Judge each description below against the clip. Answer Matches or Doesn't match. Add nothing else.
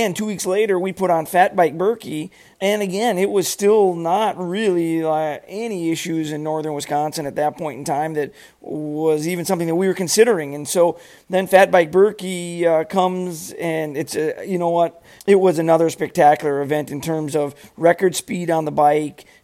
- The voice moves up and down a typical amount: Matches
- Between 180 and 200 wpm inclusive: Matches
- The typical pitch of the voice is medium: Matches